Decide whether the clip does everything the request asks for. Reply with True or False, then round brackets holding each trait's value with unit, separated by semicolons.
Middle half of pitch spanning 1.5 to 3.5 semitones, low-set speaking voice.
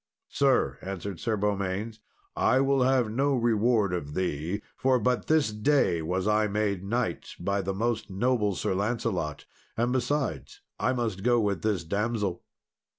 False (4.3 semitones; 105 Hz)